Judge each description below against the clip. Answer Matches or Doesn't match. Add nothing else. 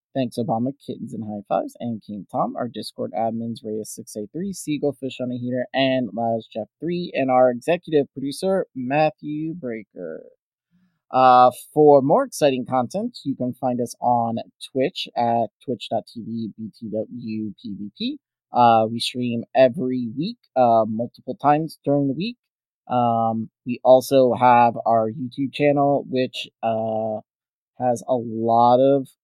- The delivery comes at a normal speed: Doesn't match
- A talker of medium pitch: Doesn't match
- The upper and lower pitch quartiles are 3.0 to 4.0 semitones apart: Matches